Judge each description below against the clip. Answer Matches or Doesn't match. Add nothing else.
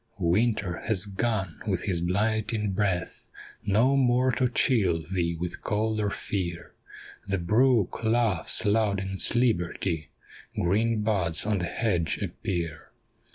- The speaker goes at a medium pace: Doesn't match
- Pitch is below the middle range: Matches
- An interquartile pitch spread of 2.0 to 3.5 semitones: Doesn't match